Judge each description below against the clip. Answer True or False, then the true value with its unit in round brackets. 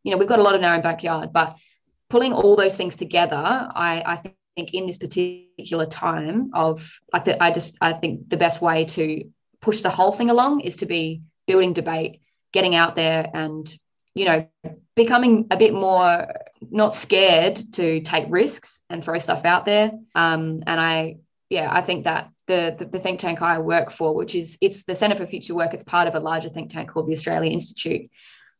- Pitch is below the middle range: False (175 Hz)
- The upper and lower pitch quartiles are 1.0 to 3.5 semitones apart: True (2.8 semitones)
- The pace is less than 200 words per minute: False (205 wpm)